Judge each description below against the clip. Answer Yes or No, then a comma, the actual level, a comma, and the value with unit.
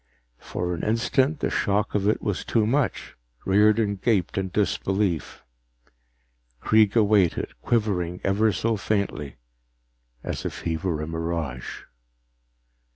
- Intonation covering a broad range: No, average, 3.6 semitones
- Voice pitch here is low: Yes, low, 100 Hz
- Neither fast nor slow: No, slow, 120 wpm